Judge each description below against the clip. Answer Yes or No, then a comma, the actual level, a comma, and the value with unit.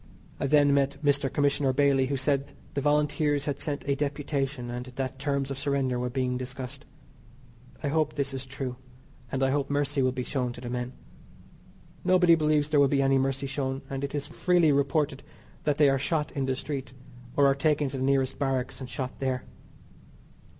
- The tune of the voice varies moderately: No, narrow, 1.6 semitones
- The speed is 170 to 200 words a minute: Yes, average, 195 wpm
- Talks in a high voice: No, medium, 140 Hz